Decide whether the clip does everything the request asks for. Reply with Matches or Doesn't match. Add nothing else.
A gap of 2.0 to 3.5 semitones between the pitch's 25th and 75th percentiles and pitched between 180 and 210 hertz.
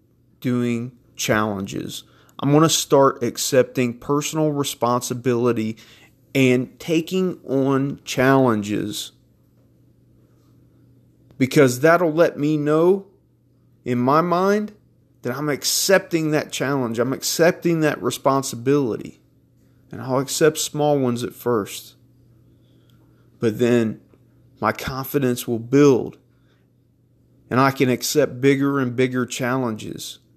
Doesn't match